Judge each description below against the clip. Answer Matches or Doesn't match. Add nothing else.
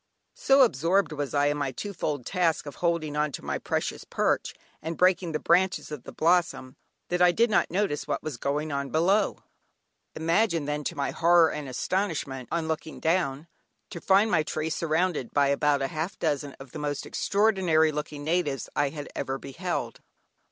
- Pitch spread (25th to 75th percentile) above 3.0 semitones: Matches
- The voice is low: Doesn't match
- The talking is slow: Doesn't match